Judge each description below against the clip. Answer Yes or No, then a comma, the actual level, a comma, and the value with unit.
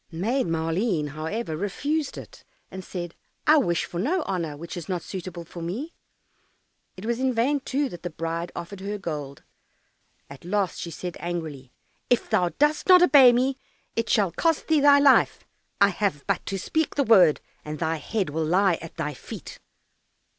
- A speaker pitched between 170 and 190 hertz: Yes, medium, 185 Hz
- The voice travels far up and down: Yes, wide, 7.3 semitones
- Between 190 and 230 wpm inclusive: No, average, 180 wpm